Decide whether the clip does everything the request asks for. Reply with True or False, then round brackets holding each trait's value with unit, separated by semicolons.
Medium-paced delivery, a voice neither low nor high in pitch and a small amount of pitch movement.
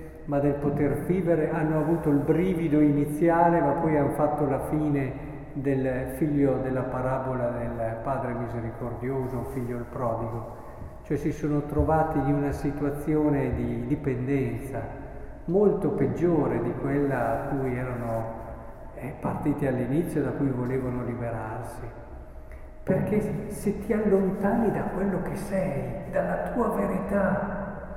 False (125 wpm; 145 Hz; 4.4 semitones)